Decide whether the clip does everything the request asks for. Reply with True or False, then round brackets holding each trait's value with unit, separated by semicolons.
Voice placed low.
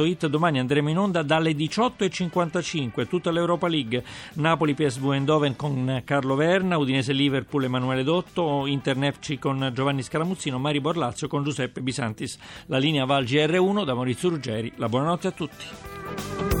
False (145 Hz)